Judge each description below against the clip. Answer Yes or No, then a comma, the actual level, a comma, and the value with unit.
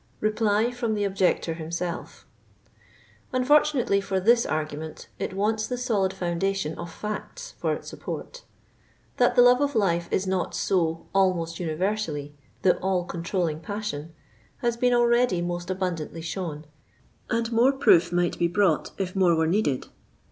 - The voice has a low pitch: No, high, 190 Hz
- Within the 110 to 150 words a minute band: Yes, average, 145 wpm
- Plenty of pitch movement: No, average, 4.7 semitones